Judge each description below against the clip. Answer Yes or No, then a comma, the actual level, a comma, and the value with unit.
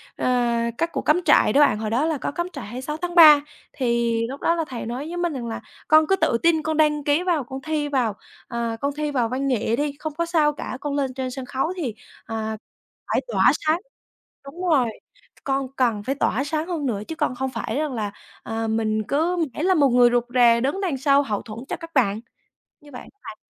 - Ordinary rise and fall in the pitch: Yes, average, 4.7 semitones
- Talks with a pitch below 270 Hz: No, very high, 275 Hz